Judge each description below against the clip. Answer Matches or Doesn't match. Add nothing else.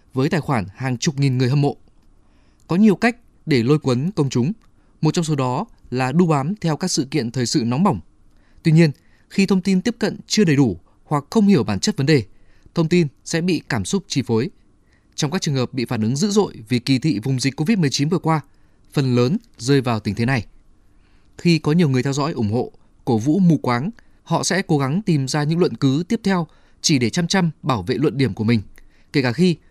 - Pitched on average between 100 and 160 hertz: Matches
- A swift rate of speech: Doesn't match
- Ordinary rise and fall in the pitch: Doesn't match